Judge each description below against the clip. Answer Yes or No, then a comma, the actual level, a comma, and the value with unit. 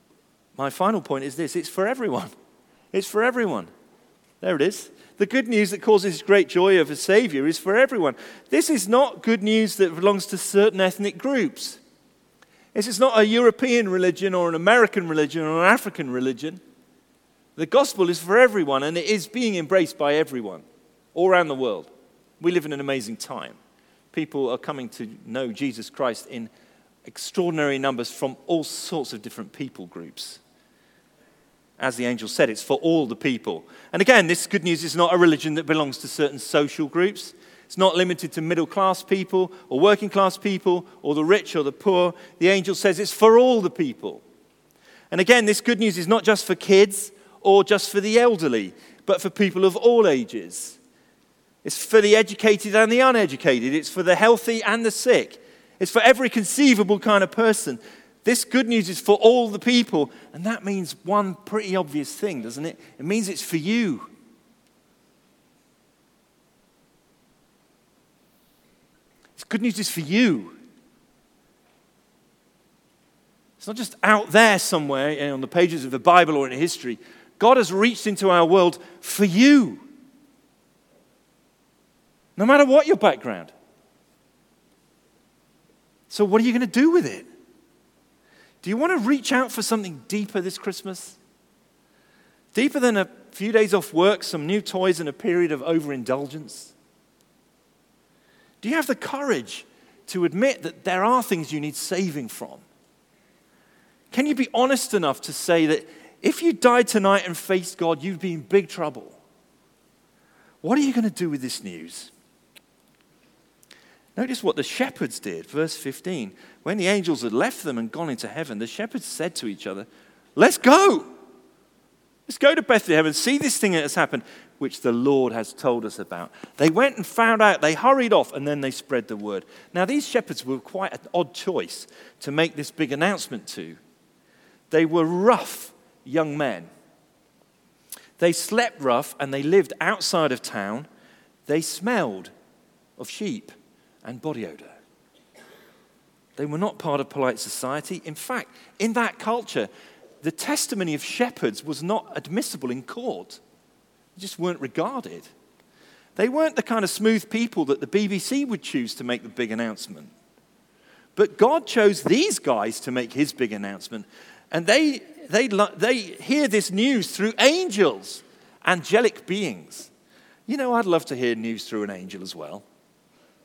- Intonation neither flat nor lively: No, wide, 6.4 semitones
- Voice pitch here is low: No, high, 195 Hz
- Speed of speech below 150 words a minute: No, average, 165 wpm